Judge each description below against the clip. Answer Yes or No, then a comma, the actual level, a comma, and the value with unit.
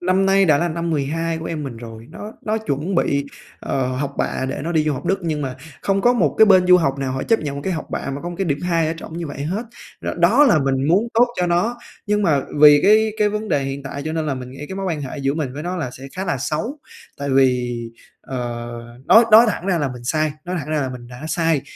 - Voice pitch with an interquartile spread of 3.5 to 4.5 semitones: No, average, 5.2 semitones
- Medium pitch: Yes, medium, 160 Hz